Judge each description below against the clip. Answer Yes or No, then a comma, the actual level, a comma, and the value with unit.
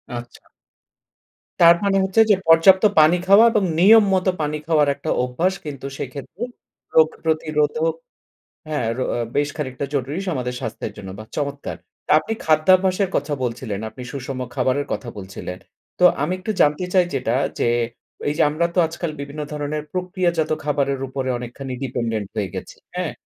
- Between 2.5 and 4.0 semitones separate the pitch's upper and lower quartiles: No, average, 5.1 semitones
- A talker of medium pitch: Yes, medium, 150 Hz